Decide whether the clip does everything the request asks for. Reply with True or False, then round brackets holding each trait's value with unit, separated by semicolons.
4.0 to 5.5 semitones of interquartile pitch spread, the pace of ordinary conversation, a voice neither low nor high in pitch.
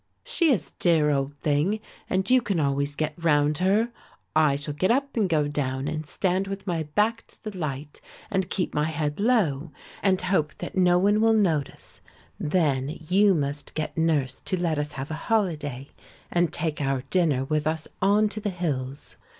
True (4.7 semitones; 190 wpm; 160 Hz)